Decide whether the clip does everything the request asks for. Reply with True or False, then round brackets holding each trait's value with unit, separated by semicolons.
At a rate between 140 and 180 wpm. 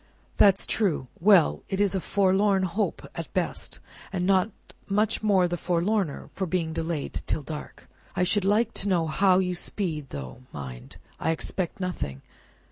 True (160 wpm)